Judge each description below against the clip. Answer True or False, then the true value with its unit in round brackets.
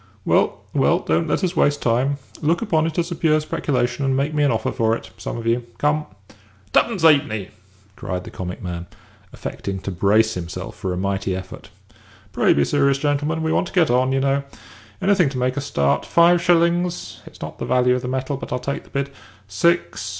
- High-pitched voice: False (135 Hz)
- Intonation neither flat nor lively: False (6.2 semitones)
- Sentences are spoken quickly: True (210 wpm)